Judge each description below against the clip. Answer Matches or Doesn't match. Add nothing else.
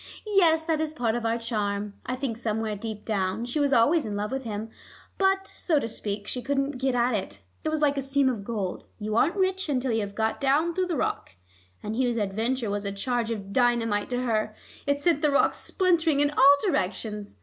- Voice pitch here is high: Matches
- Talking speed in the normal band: Doesn't match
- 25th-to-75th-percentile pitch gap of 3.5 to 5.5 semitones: Matches